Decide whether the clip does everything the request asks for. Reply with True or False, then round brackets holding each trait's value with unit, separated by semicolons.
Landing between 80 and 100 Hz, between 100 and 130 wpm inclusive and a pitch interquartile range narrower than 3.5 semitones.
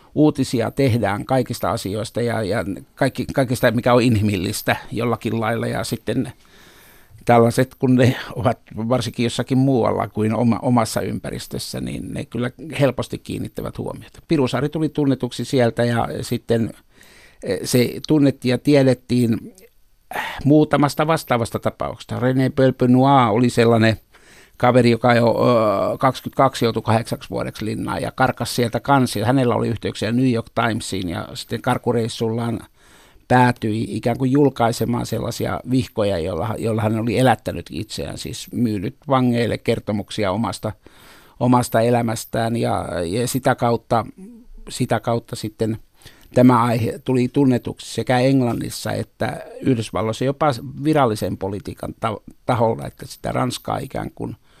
False (120 Hz; 120 wpm; 2.4 semitones)